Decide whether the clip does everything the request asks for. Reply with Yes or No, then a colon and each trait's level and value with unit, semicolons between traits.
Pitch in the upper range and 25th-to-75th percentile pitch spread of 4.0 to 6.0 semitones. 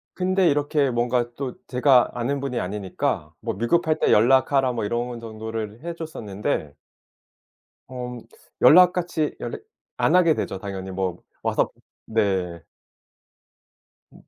No: low, 120 Hz; wide, 5.6 semitones